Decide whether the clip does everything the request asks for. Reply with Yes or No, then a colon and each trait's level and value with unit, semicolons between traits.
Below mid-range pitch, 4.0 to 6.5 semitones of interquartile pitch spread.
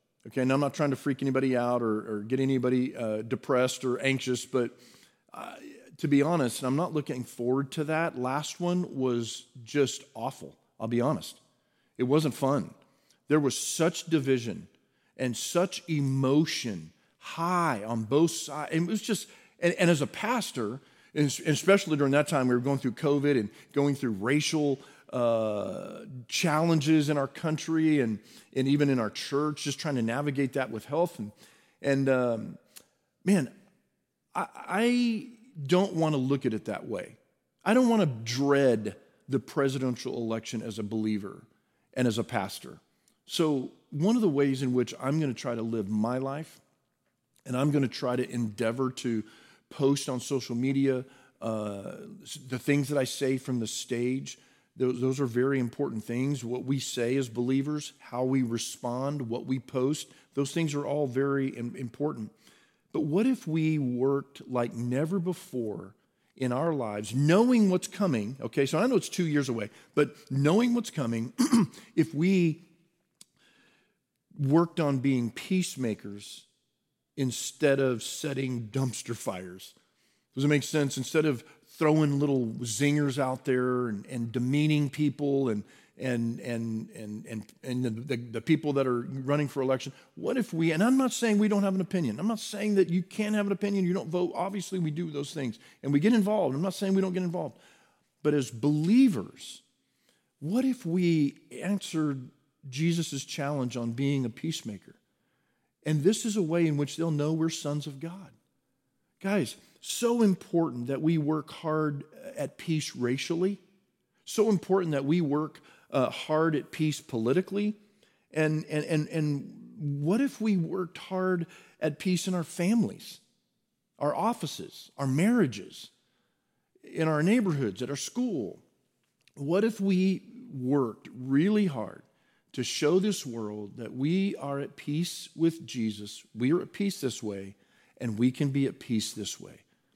No: medium, 145 Hz; average, 5.2 semitones